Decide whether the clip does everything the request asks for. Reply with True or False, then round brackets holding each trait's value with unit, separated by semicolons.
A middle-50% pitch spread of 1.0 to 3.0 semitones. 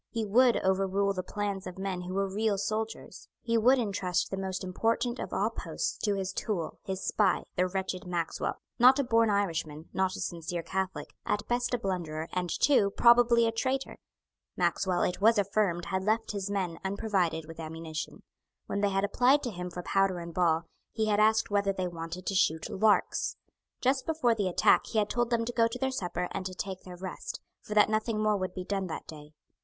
False (3.5 semitones)